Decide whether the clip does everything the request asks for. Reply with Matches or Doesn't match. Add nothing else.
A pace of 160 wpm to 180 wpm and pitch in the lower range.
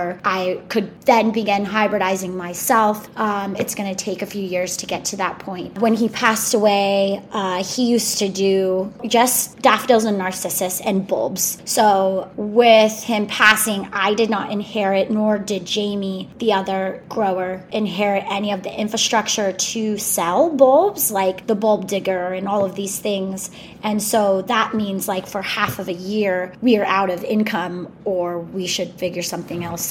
Doesn't match